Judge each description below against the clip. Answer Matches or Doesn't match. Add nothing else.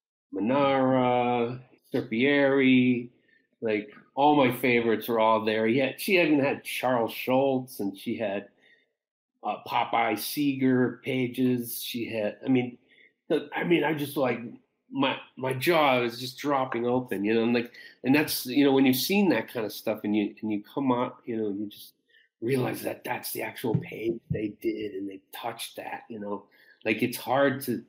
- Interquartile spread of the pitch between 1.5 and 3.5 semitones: Matches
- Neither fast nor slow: Matches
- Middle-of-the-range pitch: Doesn't match